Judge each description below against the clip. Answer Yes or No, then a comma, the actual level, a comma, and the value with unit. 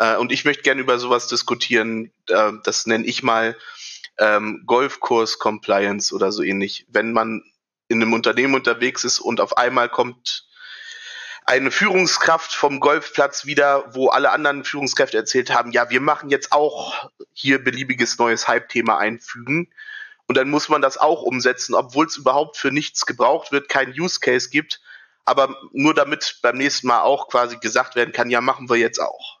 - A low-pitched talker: Yes, low, 125 Hz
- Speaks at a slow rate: No, average, 170 wpm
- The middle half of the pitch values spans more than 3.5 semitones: Yes, average, 4.2 semitones